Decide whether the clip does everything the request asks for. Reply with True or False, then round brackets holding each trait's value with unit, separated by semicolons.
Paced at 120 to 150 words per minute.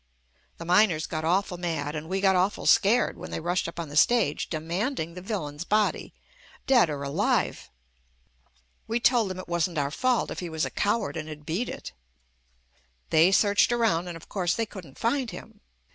False (190 wpm)